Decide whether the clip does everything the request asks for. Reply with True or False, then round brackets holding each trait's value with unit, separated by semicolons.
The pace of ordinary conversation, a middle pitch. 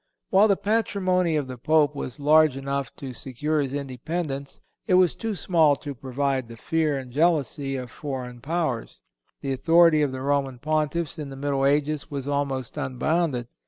True (175 wpm; 145 Hz)